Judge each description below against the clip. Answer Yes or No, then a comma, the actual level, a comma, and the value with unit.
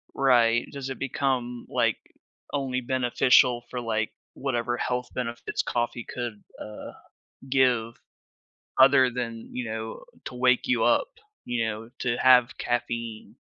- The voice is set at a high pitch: No, low, 120 Hz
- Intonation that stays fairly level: Yes, narrow, 1.6 semitones